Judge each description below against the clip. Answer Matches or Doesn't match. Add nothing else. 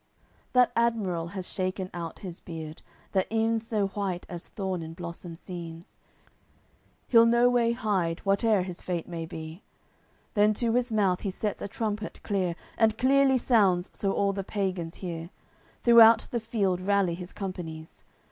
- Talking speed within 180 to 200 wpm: Doesn't match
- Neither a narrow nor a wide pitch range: Matches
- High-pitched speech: Matches